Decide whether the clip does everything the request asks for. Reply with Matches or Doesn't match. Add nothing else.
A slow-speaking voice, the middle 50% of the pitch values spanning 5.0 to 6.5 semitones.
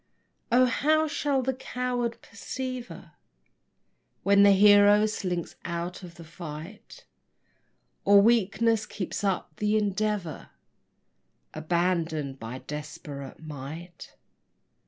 Matches